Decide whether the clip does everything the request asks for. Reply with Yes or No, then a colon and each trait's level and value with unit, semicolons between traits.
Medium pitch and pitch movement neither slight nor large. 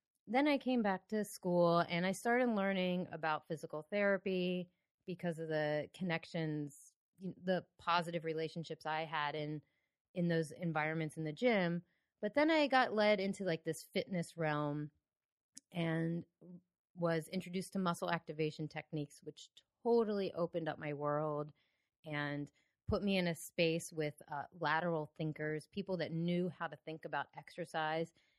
Yes: medium, 170 Hz; average, 3.2 semitones